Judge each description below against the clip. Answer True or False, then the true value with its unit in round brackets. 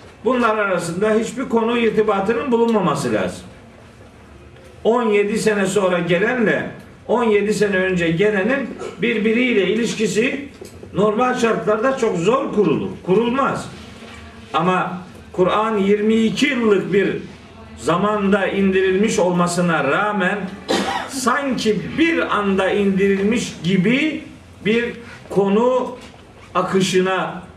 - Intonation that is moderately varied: True (3.5 semitones)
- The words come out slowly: True (85 wpm)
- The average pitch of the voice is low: False (210 Hz)